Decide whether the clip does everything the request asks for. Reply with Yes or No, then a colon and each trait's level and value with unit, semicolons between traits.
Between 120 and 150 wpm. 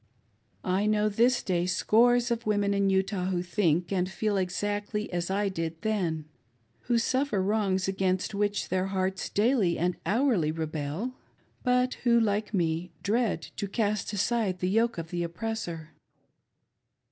Yes: average, 145 wpm